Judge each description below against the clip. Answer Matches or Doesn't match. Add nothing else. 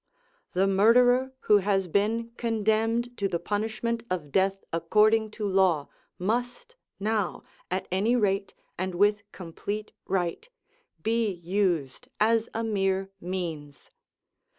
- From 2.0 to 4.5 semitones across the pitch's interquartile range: Matches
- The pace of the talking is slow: Matches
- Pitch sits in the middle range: Doesn't match